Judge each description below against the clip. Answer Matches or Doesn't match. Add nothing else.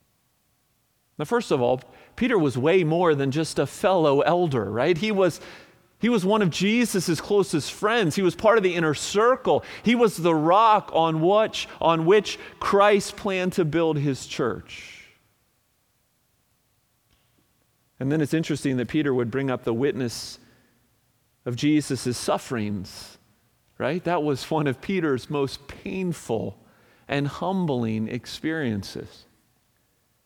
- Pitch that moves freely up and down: Matches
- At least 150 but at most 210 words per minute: Doesn't match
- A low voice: Doesn't match